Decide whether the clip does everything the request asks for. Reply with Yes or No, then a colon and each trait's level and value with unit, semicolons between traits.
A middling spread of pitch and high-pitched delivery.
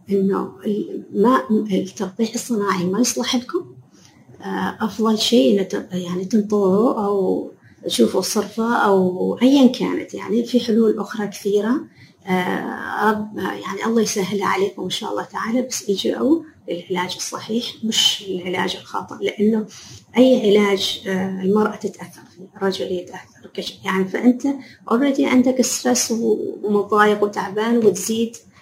Yes: average, 3.3 semitones; high, 210 Hz